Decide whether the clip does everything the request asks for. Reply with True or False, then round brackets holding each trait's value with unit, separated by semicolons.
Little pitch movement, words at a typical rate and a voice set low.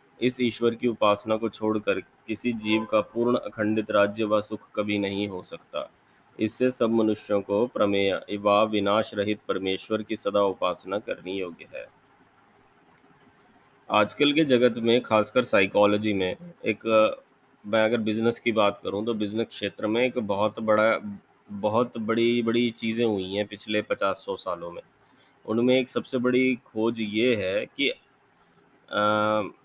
True (2.2 semitones; 150 wpm; 110 Hz)